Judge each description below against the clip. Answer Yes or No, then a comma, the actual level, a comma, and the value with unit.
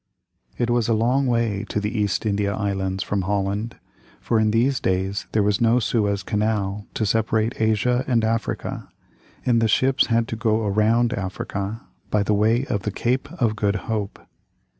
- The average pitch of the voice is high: No, low, 110 Hz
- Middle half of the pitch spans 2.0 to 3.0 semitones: Yes, narrow, 2.4 semitones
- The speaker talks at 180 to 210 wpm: No, average, 170 wpm